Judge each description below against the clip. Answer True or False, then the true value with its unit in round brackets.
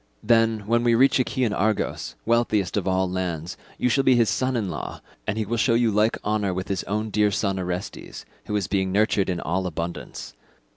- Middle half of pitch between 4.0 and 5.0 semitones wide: False (3.5 semitones)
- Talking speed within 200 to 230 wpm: True (205 wpm)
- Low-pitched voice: True (105 Hz)